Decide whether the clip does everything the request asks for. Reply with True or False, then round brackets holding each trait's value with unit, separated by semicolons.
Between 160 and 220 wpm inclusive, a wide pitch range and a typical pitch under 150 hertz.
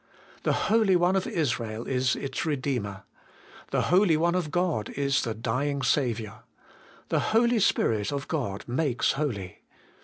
False (145 wpm; 6.8 semitones; 140 Hz)